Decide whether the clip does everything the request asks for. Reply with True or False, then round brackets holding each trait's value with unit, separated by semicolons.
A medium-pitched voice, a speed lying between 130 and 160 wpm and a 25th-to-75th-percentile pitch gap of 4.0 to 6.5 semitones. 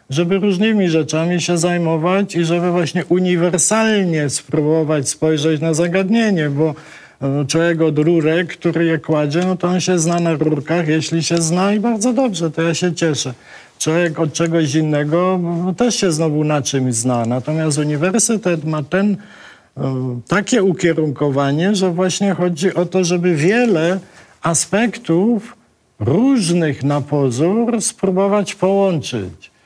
False (170 Hz; 135 wpm; 3.1 semitones)